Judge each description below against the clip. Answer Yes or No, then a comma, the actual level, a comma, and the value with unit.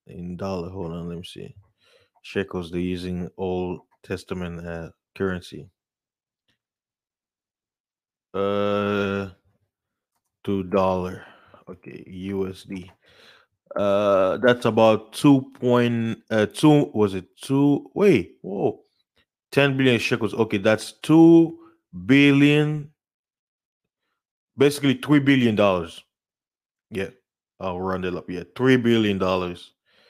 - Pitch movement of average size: No, wide, 6.0 semitones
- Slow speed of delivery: Yes, slow, 100 wpm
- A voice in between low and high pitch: No, low, 100 Hz